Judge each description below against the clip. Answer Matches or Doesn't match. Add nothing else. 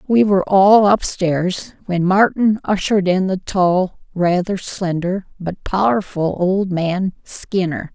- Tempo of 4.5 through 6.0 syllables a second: Doesn't match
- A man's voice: Doesn't match